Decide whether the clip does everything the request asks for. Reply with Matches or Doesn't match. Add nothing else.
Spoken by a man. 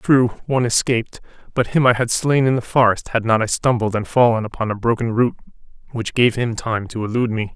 Matches